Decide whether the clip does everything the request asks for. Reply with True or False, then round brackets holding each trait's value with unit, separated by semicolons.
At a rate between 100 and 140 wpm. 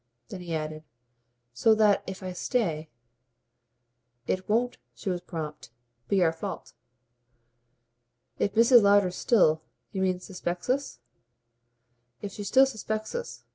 True (135 wpm)